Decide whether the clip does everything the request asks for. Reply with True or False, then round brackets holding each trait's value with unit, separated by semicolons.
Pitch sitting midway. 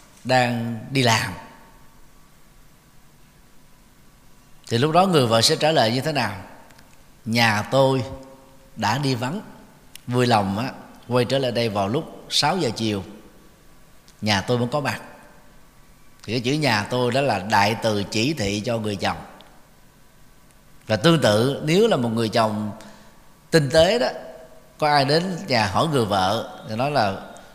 False (125 Hz)